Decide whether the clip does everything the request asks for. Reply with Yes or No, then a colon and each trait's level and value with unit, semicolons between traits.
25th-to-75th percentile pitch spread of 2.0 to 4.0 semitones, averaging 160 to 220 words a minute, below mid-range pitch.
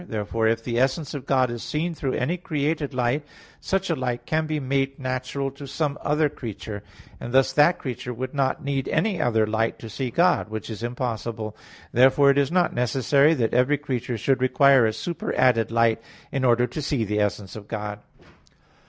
Yes: average, 3.7 semitones; average, 190 wpm; low, 130 Hz